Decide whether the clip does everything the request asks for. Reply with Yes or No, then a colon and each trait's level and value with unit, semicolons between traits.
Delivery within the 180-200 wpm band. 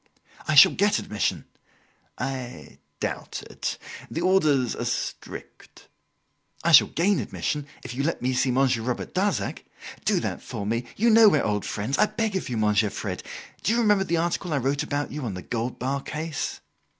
Yes: average, 185 wpm